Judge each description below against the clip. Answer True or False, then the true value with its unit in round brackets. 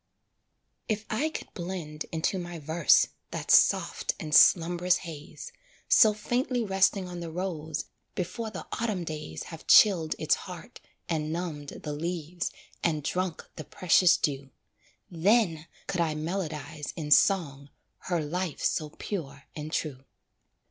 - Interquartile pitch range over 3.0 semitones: True (3.4 semitones)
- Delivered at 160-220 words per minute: False (135 wpm)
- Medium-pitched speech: True (170 Hz)